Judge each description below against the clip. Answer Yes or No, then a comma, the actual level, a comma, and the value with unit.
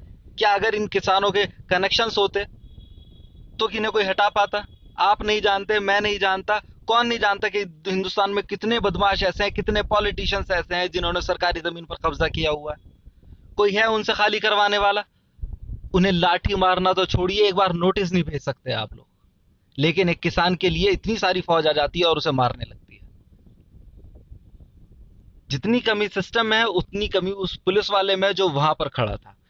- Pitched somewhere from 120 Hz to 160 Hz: No, high, 190 Hz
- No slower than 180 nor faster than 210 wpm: Yes, average, 185 wpm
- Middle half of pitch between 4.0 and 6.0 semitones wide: Yes, average, 5.0 semitones